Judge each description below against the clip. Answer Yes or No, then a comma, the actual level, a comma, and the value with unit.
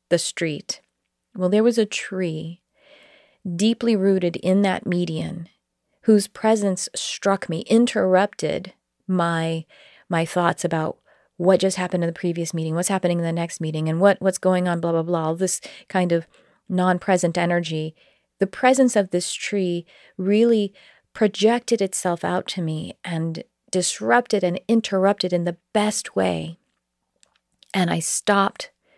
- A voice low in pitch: No, medium, 185 Hz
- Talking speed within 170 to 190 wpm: No, average, 145 wpm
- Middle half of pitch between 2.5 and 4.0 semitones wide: Yes, average, 3.0 semitones